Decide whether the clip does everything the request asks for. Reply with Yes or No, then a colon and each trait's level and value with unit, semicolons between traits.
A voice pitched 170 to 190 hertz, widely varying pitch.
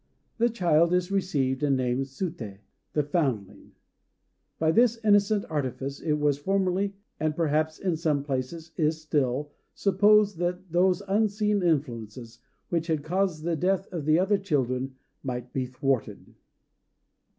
No: medium, 160 Hz; wide, 5.7 semitones